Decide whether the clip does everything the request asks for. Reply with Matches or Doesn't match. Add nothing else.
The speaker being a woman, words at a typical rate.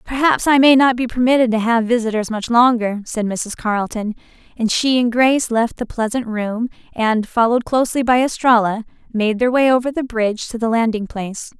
Matches